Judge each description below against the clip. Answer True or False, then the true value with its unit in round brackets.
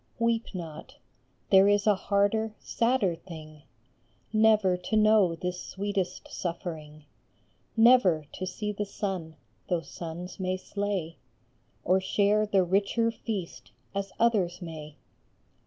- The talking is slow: True (120 wpm)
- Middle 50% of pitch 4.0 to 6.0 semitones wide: False (3.3 semitones)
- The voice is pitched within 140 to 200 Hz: True (190 Hz)